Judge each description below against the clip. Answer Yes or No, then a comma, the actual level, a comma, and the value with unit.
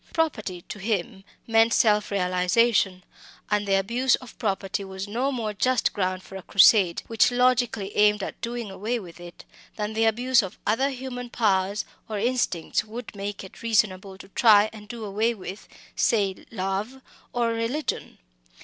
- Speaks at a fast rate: No, average, 160 wpm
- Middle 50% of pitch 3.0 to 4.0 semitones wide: Yes, average, 3.5 semitones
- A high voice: Yes, high, 210 Hz